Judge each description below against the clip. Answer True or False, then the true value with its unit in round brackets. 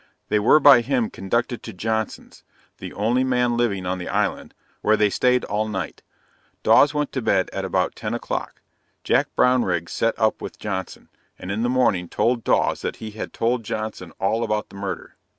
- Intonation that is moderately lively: True (3.8 semitones)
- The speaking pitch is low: True (110 Hz)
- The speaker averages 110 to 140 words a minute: False (185 wpm)